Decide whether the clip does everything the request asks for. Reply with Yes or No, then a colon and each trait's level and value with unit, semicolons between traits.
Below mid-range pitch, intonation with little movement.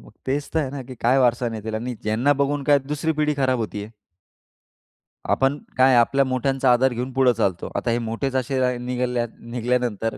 Yes: low, 125 Hz; narrow, 2.3 semitones